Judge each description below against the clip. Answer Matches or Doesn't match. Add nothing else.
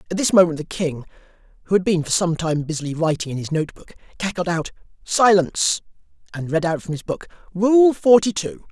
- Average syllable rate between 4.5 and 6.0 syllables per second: Matches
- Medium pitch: Matches